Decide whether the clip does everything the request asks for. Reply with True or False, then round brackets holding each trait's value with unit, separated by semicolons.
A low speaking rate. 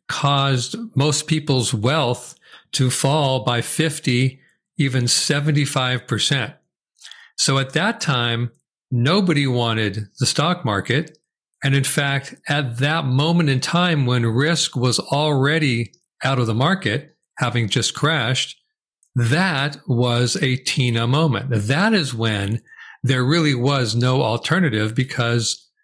True (120 wpm)